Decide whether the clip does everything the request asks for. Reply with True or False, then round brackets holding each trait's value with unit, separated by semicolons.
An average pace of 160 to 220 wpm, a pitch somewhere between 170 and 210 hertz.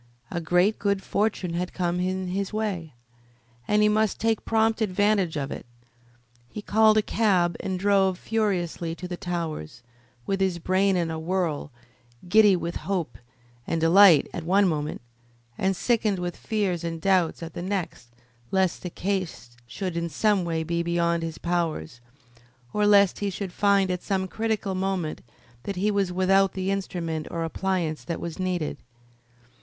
True (165 wpm; 185 Hz)